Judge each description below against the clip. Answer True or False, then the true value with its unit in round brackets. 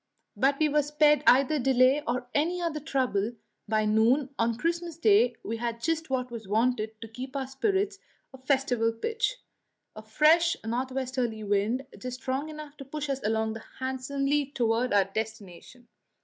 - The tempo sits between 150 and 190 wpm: True (165 wpm)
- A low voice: False (260 Hz)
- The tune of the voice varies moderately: True (4.7 semitones)